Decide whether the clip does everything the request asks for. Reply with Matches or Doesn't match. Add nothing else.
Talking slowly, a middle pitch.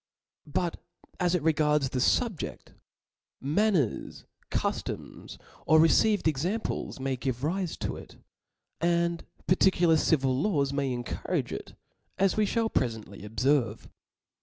Matches